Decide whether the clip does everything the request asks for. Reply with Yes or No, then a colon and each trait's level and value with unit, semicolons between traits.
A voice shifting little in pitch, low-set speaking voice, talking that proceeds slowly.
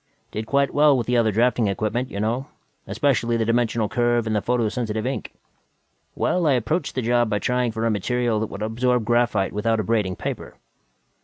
No: narrow, 2.3 semitones; low, 115 Hz; average, 185 wpm